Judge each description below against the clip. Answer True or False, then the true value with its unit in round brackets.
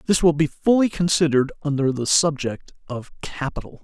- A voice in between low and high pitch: True (155 Hz)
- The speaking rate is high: False (155 wpm)